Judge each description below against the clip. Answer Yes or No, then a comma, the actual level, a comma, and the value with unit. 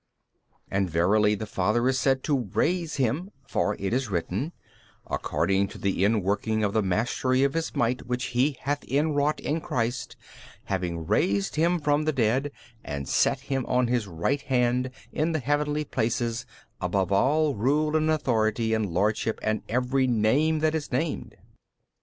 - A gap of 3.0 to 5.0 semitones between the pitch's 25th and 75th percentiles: No, wide, 5.6 semitones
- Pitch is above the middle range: No, low, 125 Hz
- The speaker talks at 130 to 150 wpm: No, average, 170 wpm